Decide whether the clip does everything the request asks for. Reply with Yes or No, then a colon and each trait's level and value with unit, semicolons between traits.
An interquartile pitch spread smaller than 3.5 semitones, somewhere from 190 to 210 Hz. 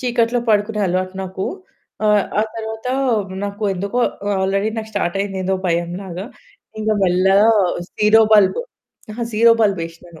Yes: average, 2.8 semitones; high, 200 Hz